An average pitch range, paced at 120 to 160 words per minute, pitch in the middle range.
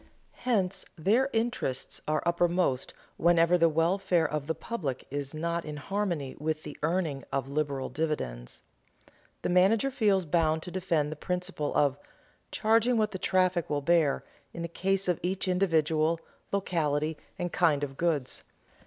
Yes: average, 3.8 semitones; average, 150 wpm; medium, 170 Hz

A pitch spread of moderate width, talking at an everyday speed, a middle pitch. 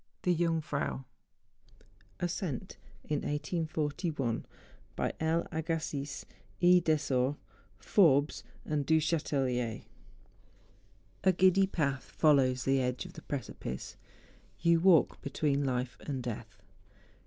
No: average, 3.9 semitones; slow, 100 wpm; medium, 150 Hz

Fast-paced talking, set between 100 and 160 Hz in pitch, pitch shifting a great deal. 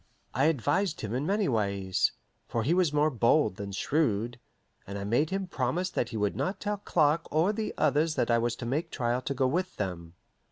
Yes: fast, 210 wpm; medium, 140 Hz; wide, 6.4 semitones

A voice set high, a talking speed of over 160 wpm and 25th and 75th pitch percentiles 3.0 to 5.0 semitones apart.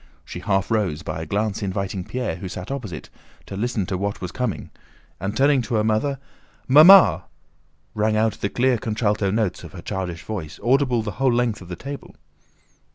No: low, 110 Hz; average, 185 wpm; average, 4.2 semitones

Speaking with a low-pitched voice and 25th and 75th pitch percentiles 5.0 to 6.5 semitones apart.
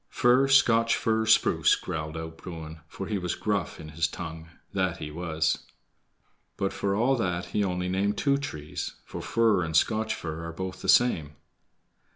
Yes: very low, 90 Hz; average, 5.3 semitones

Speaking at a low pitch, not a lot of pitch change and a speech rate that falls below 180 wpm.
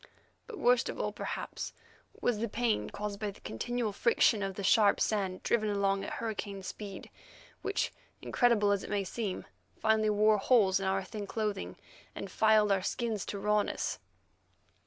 No: high, 210 Hz; narrow, 1.9 semitones; average, 165 wpm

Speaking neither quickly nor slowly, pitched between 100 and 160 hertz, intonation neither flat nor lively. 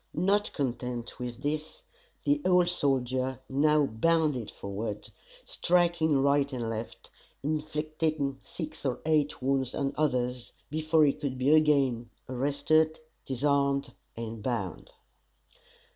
No: slow, 115 wpm; medium, 140 Hz; average, 3.7 semitones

